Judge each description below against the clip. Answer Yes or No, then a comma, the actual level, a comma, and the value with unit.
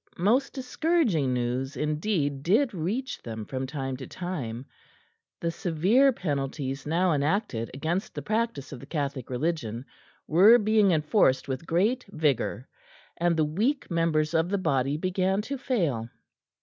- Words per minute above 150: No, average, 140 wpm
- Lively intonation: Yes, wide, 6.7 semitones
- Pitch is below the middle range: No, medium, 160 Hz